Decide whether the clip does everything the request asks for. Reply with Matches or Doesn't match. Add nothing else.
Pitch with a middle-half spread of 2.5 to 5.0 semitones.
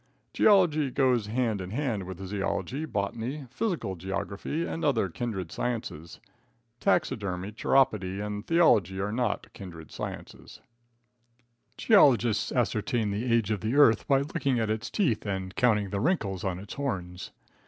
Doesn't match